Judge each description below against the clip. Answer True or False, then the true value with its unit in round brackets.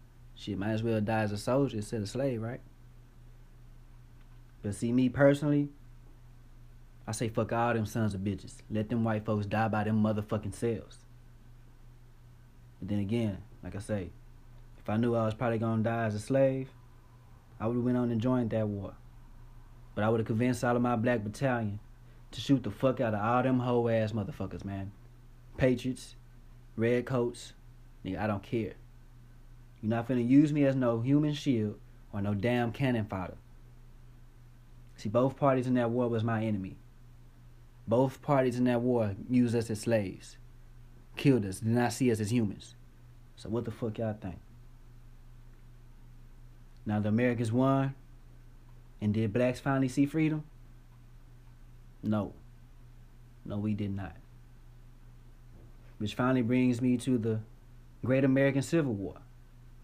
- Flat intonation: True (1.3 semitones)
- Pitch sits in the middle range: False (120 Hz)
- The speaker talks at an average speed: True (160 wpm)